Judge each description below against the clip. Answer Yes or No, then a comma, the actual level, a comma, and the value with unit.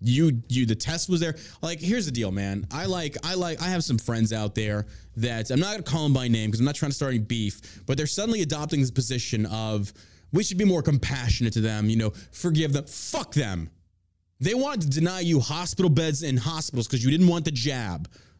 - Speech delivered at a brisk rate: Yes, fast, 235 wpm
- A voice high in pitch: No, low, 135 Hz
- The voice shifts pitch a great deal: Yes, wide, 6.6 semitones